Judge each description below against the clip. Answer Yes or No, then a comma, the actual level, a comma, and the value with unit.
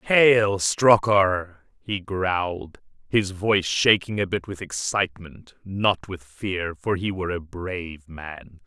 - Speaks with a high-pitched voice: No, very low, 95 Hz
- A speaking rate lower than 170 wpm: Yes, average, 140 wpm